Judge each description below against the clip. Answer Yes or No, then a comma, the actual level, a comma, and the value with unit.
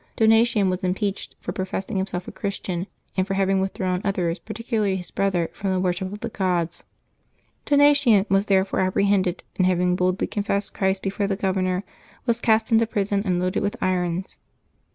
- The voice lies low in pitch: No, high, 195 Hz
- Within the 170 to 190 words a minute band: Yes, average, 175 wpm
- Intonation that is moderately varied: No, narrow, 1.9 semitones